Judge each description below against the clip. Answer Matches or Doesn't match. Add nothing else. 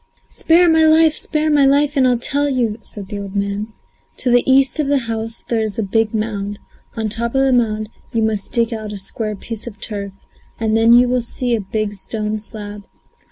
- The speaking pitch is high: Matches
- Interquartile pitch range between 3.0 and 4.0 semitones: Matches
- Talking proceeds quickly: Matches